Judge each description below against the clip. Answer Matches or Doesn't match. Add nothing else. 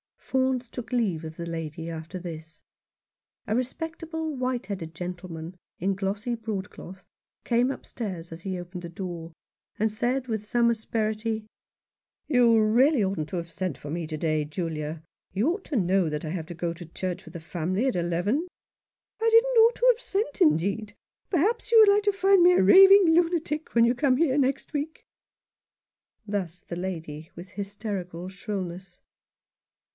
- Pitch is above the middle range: Matches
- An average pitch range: Doesn't match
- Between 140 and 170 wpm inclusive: Doesn't match